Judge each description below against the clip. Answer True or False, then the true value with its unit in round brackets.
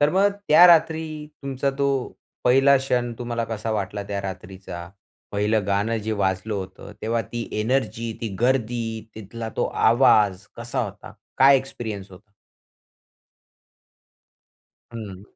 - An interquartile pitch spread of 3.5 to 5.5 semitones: True (4.6 semitones)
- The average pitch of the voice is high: False (115 Hz)